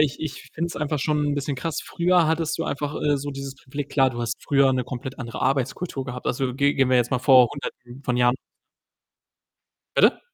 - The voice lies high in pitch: No, low, 135 Hz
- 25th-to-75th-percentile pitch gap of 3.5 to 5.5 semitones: No, narrow, 2.5 semitones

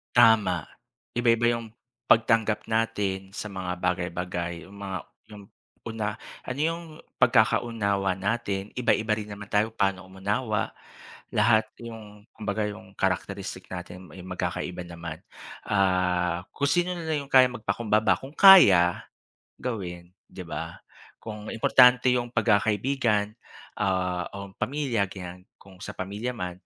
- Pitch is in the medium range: No, low, 105 Hz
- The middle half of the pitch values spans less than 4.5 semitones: Yes, average, 3.7 semitones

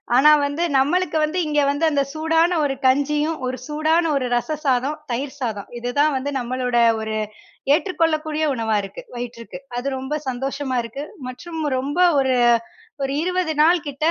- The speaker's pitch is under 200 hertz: No, very high, 285 Hz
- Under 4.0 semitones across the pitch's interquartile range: Yes, average, 3.5 semitones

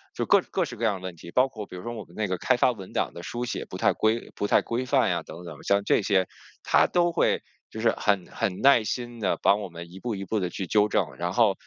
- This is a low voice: Yes, low, 105 Hz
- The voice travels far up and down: No, average, 4.3 semitones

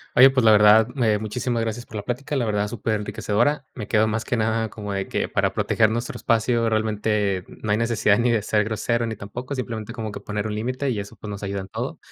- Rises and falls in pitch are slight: Yes, narrow, 2.1 semitones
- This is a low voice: Yes, low, 110 Hz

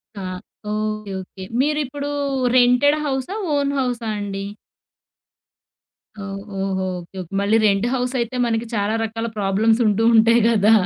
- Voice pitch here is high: Yes, high, 225 Hz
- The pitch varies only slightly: No, average, 3.7 semitones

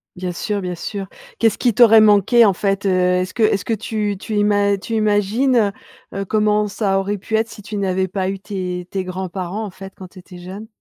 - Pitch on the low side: No, high, 200 Hz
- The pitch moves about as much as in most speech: No, narrow, 2.2 semitones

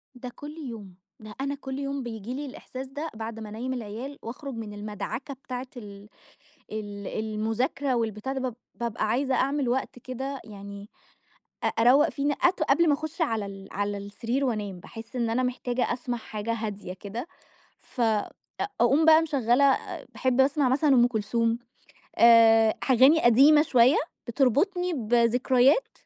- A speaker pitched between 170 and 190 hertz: No, high, 245 Hz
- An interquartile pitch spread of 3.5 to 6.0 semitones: Yes, average, 3.9 semitones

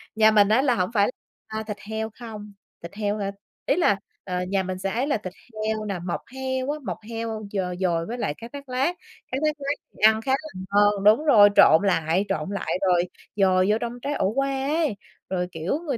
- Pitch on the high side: Yes, high, 215 Hz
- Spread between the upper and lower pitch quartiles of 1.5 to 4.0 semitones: No, average, 5.1 semitones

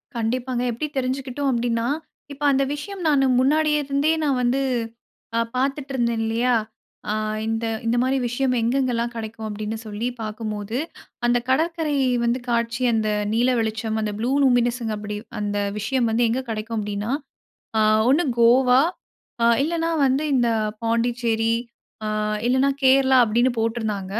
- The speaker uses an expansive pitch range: No, average, 2.9 semitones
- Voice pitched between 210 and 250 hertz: Yes, high, 240 Hz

